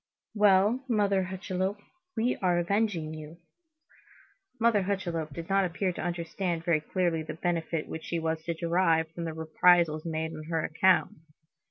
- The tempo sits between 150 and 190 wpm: Yes, average, 155 wpm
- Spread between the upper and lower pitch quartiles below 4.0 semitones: Yes, average, 2.8 semitones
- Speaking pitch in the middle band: Yes, medium, 175 Hz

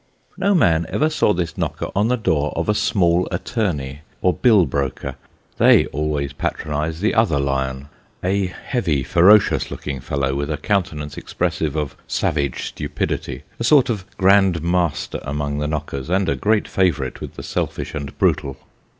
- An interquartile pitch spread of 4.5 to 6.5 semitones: Yes, wide, 5.5 semitones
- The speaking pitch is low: Yes, very low, 80 Hz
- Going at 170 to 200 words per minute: No, average, 160 wpm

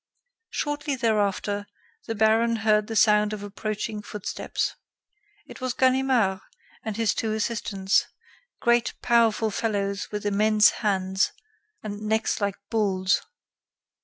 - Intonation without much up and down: Yes, narrow, 1.9 semitones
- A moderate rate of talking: No, slow, 115 wpm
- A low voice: No, high, 215 Hz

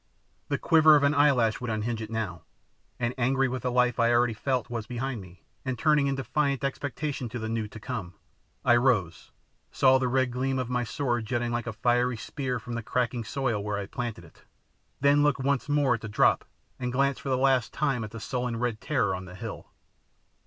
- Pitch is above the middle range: No, low, 125 Hz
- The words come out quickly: Yes, fast, 215 wpm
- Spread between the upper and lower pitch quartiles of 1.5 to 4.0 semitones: Yes, average, 3.1 semitones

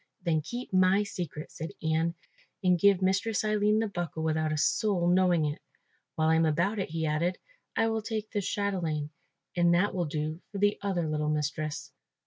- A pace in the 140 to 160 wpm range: No, average, 185 wpm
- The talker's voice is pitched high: No, medium, 175 Hz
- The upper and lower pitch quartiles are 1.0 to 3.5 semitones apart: No, average, 4.3 semitones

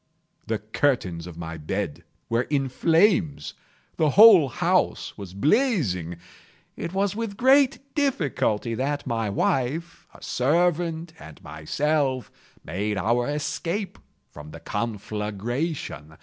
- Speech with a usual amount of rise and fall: No, wide, 8.6 semitones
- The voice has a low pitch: Yes, low, 130 Hz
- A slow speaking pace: Yes, slow, 115 wpm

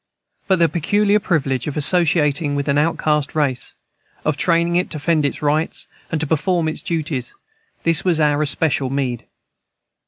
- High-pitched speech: No, medium, 155 Hz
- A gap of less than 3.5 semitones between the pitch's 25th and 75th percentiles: Yes, average, 2.8 semitones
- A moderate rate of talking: Yes, average, 160 wpm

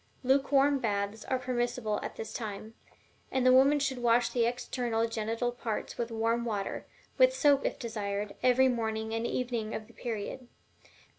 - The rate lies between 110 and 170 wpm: Yes, average, 160 wpm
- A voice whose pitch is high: Yes, high, 235 Hz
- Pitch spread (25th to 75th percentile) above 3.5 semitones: No, narrow, 2.4 semitones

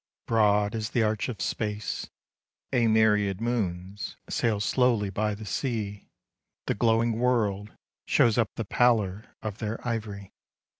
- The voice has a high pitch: No, low, 110 Hz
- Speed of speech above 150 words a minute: No, average, 140 wpm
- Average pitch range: No, narrow, 2.2 semitones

